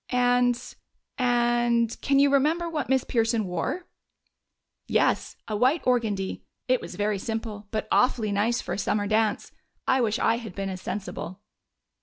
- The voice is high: Yes, high, 230 Hz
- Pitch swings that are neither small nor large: Yes, average, 3.2 semitones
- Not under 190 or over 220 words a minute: No, average, 155 wpm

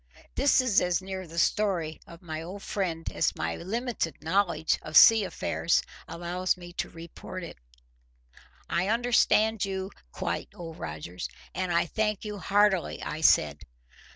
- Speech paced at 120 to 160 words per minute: Yes, average, 150 wpm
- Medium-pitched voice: Yes, medium, 180 Hz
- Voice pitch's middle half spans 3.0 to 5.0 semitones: Yes, average, 3.7 semitones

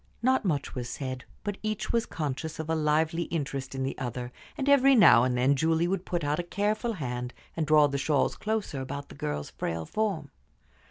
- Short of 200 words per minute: No, fast, 205 wpm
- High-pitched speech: No, medium, 155 Hz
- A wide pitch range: Yes, wide, 6.6 semitones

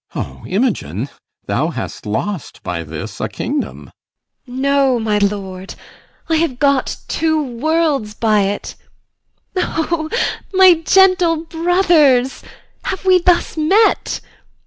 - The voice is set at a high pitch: Yes, very high, 280 Hz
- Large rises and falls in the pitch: Yes, wide, 8.3 semitones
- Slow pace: Yes, slow, 110 wpm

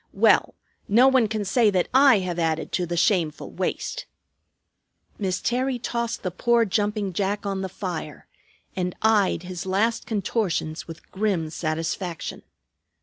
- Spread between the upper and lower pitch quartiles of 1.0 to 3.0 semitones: No, average, 4.2 semitones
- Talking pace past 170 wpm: No, average, 145 wpm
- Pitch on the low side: No, high, 195 Hz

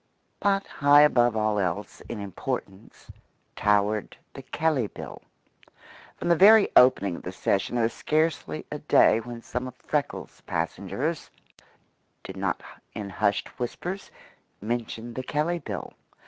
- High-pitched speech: No, low, 120 Hz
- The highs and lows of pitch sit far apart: Yes, wide, 6.3 semitones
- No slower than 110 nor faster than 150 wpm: Yes, slow, 135 wpm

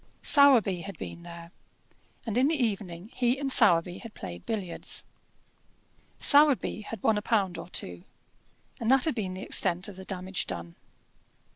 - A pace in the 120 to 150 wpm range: No, average, 160 wpm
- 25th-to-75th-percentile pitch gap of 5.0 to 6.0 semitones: Yes, average, 5.3 semitones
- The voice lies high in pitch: Yes, high, 200 Hz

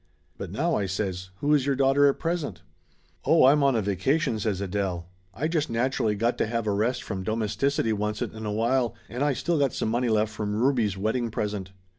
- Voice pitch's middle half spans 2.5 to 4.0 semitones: No, average, 4.7 semitones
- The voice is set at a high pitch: No, low, 115 Hz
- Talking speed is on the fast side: Yes, fast, 220 wpm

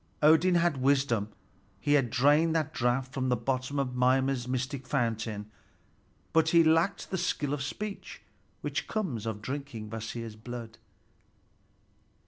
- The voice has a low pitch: Yes, low, 130 Hz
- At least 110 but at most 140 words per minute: Yes, slow, 135 wpm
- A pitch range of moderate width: Yes, average, 3.8 semitones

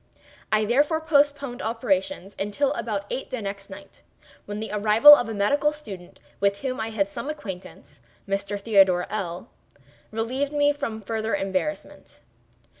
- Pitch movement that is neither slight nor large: No, wide, 6.0 semitones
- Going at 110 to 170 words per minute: Yes, average, 145 wpm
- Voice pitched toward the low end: No, high, 220 Hz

